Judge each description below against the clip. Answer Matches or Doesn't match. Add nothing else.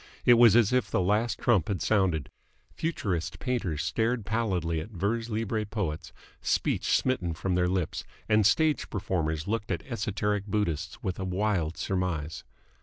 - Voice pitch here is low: Matches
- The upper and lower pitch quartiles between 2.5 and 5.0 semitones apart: Matches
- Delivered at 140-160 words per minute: Matches